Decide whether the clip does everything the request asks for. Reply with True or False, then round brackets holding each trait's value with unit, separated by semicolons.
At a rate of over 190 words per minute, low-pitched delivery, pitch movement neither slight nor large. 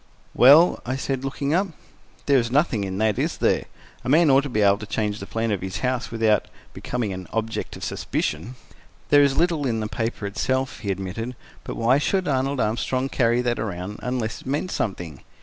True (200 wpm; 120 Hz; 4.2 semitones)